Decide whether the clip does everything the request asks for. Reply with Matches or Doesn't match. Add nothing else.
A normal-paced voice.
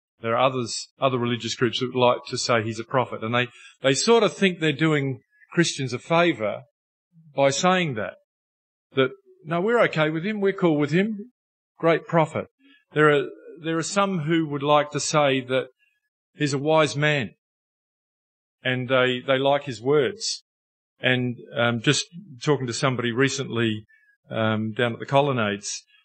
Matches